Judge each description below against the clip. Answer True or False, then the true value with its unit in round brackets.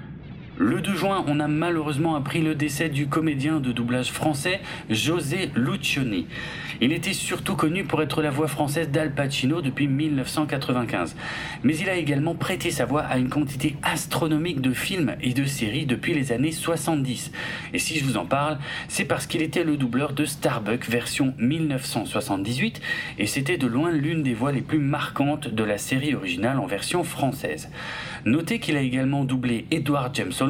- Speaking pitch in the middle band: True (150 Hz)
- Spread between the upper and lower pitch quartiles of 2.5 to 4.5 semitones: True (3.5 semitones)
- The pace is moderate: True (175 wpm)